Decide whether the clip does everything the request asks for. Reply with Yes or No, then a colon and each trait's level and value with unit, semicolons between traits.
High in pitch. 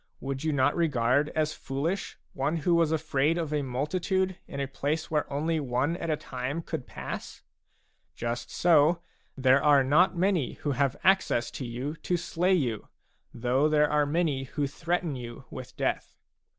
No: medium, 150 Hz